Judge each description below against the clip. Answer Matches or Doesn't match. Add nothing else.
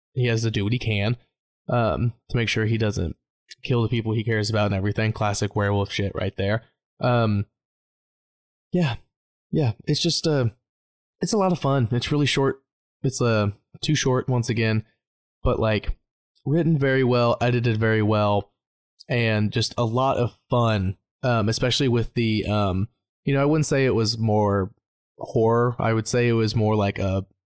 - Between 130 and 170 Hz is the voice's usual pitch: Doesn't match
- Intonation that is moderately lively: Matches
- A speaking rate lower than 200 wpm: Matches